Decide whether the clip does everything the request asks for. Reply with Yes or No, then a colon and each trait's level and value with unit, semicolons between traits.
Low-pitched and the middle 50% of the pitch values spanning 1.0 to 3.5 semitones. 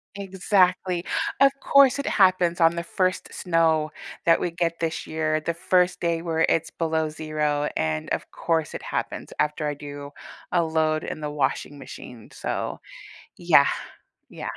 No: medium, 165 Hz; narrow, 2.6 semitones